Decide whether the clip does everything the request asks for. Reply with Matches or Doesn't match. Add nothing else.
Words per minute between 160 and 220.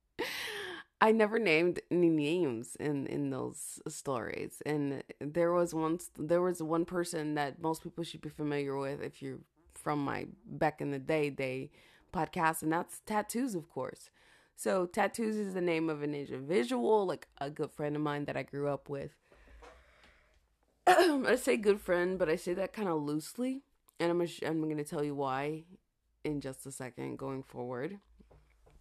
Matches